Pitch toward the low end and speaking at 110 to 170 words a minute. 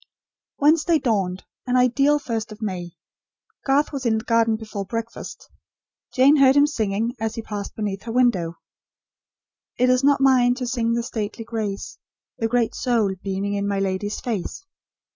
No: high, 230 Hz; average, 160 wpm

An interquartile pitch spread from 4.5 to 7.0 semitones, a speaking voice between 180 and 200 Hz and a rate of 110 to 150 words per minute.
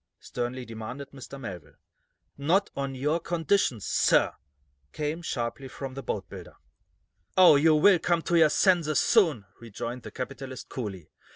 No: average, 5.3 semitones; low, 135 Hz; slow, 135 wpm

